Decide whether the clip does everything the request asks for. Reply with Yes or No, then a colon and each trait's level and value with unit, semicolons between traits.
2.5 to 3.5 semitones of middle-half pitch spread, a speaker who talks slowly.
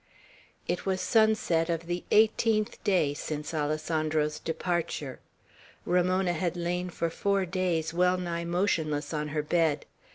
Yes: average, 2.9 semitones; slow, 130 wpm